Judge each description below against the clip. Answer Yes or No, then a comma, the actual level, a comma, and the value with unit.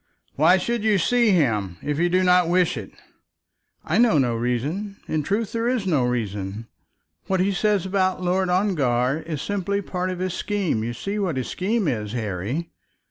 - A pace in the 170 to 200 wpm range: Yes, average, 190 wpm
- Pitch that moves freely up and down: Yes, wide, 8.0 semitones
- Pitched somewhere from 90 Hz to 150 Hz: No, medium, 180 Hz